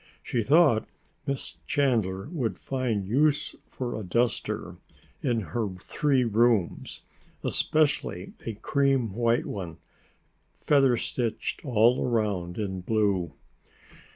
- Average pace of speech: No, slow, 105 wpm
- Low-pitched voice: Yes, low, 115 Hz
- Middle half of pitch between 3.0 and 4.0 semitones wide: No, average, 4.7 semitones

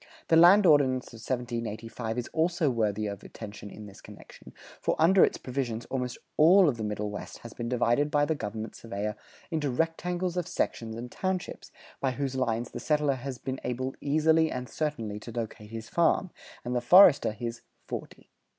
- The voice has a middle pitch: No, low, 125 Hz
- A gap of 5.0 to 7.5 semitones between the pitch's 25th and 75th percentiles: Yes, wide, 5.5 semitones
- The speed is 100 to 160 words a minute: No, average, 180 wpm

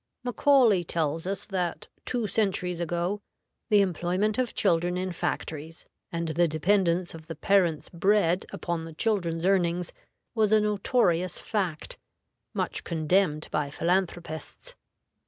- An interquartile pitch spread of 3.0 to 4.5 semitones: Yes, average, 3.5 semitones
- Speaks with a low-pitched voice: No, medium, 175 Hz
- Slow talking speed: Yes, slow, 125 wpm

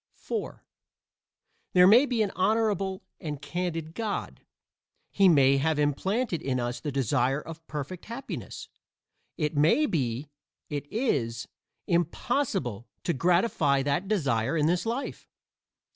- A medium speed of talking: No, slow, 125 wpm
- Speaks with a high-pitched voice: No, medium, 160 Hz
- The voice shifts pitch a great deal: Yes, wide, 6.1 semitones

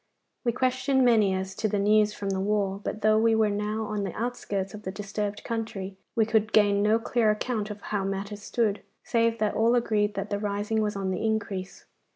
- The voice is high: Yes, high, 210 Hz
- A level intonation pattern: Yes, narrow, 1.7 semitones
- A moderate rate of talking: No, fast, 210 wpm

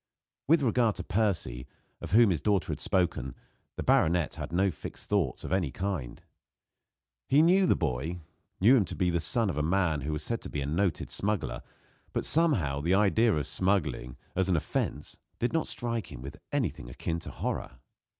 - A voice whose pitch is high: No, very low, 90 Hz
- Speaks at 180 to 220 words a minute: Yes, average, 190 wpm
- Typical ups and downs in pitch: No, wide, 6.3 semitones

